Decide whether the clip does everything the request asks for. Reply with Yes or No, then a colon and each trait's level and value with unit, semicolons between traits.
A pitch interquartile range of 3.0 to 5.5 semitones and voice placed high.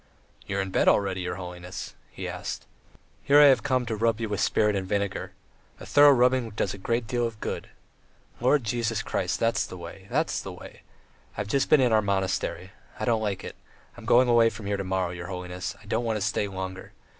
No: average, 3.8 semitones; low, 105 Hz